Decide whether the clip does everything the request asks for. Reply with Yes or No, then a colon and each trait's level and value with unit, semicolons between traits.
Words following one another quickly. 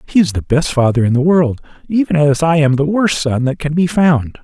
Yes: fast, 255 wpm